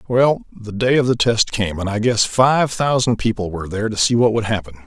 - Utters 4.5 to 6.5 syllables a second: Yes, 5.6 syllables/s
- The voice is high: No, low, 115 Hz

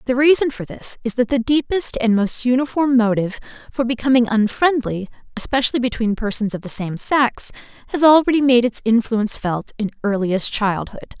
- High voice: Yes, high, 240 Hz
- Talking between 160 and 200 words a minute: Yes, average, 165 wpm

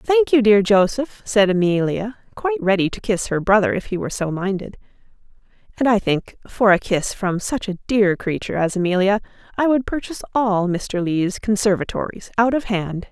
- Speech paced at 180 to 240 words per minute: Yes, average, 185 wpm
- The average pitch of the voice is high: Yes, high, 205 Hz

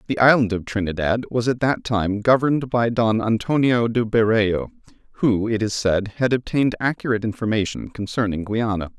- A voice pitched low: Yes, low, 115 Hz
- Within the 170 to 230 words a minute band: No, average, 160 wpm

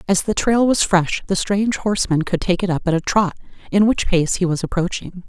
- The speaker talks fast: Yes, fast, 225 wpm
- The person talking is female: Yes, female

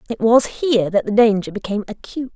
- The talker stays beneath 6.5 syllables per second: No, 6.6 syllables/s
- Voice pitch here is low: No, high, 220 Hz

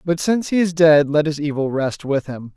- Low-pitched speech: No, medium, 155 Hz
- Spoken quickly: Yes, fast, 260 wpm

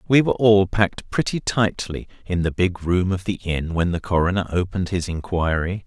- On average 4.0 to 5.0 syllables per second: No, 5.3 syllables/s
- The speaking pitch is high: No, very low, 95 Hz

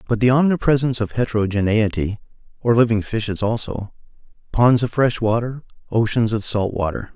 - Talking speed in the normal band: No, slow, 125 wpm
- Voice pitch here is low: Yes, low, 115 Hz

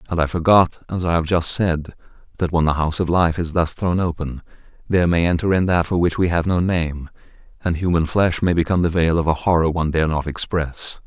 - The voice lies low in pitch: Yes, very low, 85 Hz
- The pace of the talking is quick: Yes, fast, 235 wpm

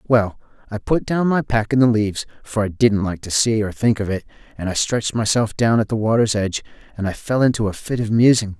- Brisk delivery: Yes, fast, 260 wpm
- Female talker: No, male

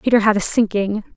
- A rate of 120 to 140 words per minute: No, fast, 205 wpm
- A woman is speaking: Yes, female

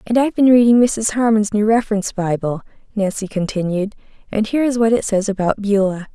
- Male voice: No, female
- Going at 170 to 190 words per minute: Yes, average, 185 wpm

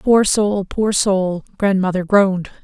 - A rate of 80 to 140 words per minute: Yes, slow, 135 wpm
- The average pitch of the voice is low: No, high, 195 Hz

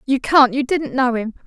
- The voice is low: No, very high, 260 Hz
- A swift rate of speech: Yes, fast, 245 wpm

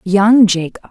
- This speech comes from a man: No, female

